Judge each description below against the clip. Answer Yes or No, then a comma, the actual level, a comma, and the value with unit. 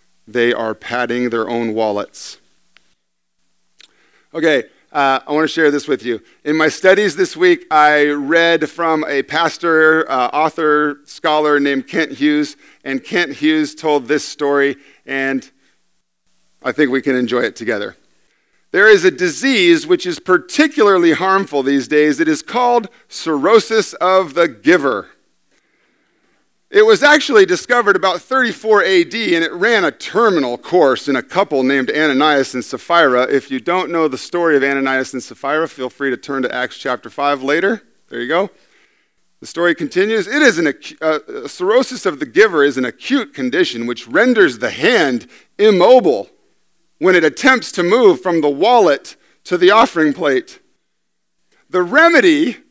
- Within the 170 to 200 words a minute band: No, average, 160 wpm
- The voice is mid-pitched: Yes, medium, 155 Hz